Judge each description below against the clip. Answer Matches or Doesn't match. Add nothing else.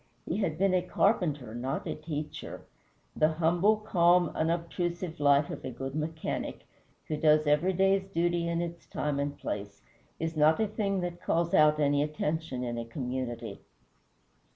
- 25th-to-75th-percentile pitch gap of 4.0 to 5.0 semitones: Doesn't match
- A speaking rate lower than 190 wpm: Matches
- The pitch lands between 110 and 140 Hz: Doesn't match